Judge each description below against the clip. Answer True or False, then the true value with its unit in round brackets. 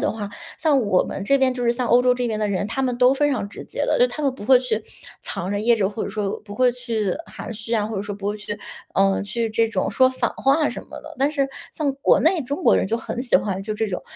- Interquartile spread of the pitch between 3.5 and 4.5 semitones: True (3.9 semitones)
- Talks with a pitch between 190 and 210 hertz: False (230 Hz)